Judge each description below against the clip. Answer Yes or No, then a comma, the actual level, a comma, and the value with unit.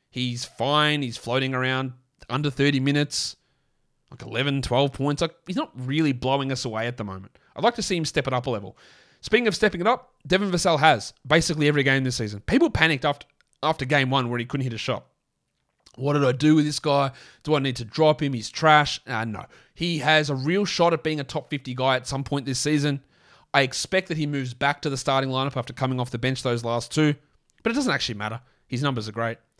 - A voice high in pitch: No, medium, 140 Hz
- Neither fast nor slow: No, fast, 235 wpm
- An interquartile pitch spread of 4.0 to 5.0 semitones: No, average, 3.2 semitones